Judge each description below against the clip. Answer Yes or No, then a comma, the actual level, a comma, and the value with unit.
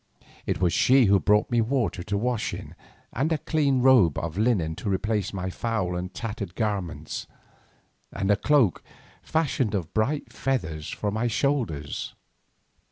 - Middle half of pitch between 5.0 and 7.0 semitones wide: Yes, average, 5.3 semitones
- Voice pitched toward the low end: Yes, low, 105 Hz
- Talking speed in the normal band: Yes, average, 155 wpm